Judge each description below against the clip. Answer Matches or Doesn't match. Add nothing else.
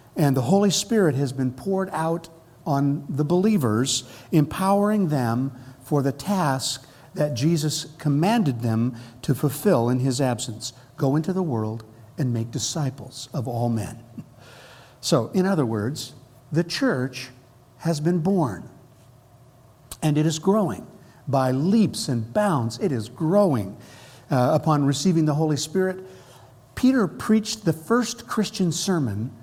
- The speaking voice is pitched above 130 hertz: Matches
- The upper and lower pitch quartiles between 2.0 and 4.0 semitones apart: Doesn't match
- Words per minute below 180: Matches